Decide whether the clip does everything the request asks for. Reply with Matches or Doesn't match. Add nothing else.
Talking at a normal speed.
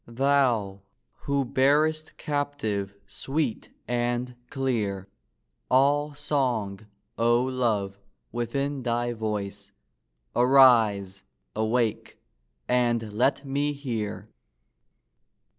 Doesn't match